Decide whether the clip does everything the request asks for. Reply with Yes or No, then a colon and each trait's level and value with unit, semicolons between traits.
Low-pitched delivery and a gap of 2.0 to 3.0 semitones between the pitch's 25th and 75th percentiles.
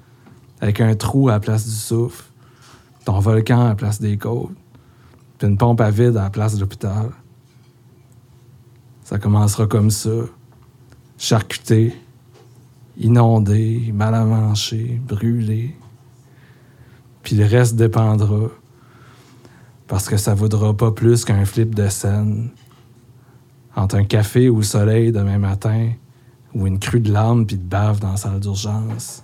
Yes: low, 115 Hz; narrow, 2.5 semitones